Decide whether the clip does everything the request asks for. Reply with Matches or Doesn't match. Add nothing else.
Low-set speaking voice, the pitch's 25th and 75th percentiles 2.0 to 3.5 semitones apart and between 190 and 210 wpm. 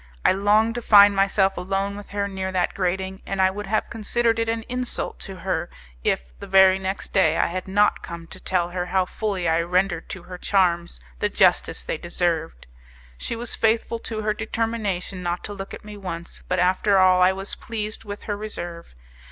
Doesn't match